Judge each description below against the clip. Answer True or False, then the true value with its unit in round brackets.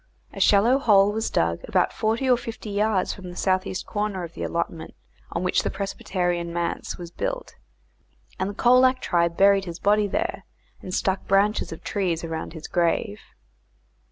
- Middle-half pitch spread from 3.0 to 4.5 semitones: True (3.5 semitones)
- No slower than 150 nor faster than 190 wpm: True (175 wpm)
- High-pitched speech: True (195 Hz)